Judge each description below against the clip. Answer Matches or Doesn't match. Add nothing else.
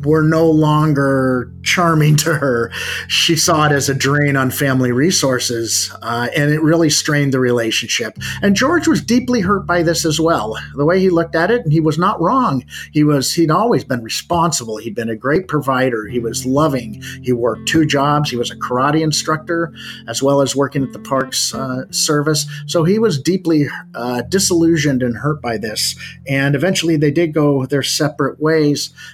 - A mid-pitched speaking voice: Matches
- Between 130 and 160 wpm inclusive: Doesn't match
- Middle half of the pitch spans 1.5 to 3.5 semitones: Doesn't match